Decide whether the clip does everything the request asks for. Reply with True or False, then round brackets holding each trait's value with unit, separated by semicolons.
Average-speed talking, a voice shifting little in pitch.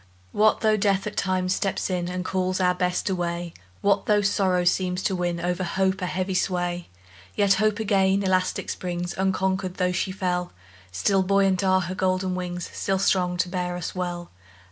True (180 wpm; 1.3 semitones)